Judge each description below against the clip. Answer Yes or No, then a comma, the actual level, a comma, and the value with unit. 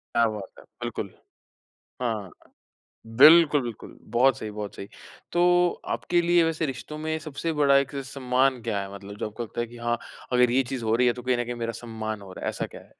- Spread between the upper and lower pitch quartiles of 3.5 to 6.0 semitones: Yes, average, 4.5 semitones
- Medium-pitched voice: No, low, 125 Hz